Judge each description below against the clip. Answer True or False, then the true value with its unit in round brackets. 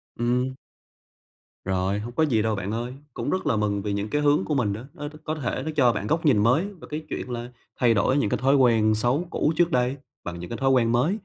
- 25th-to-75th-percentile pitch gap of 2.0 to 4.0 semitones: False (5.3 semitones)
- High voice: False (125 Hz)